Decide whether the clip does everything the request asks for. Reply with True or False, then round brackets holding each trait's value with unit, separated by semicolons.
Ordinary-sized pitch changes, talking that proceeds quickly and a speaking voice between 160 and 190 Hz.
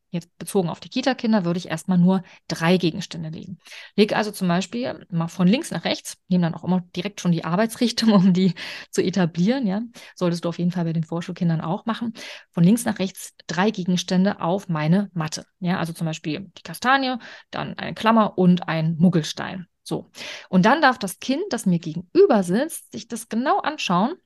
True (3.9 semitones; 195 wpm; 185 Hz)